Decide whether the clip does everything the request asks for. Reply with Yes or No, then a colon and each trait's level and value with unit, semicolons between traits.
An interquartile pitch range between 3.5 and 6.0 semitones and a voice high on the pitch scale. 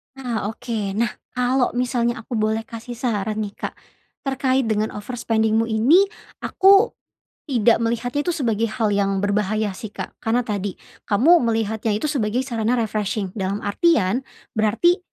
No: average, 2.9 semitones; high, 225 Hz